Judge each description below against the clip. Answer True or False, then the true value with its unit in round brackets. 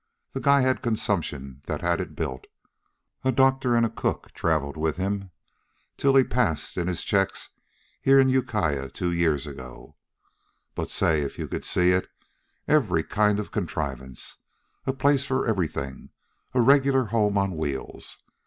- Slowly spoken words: False (160 wpm)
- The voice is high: False (100 Hz)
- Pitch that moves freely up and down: True (8.8 semitones)